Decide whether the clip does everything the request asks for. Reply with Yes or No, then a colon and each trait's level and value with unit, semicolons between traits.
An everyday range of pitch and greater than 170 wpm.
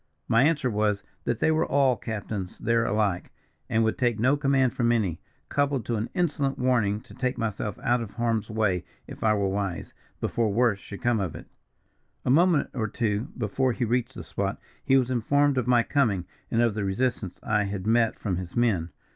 Yes: average, 3.6 semitones; average, 200 wpm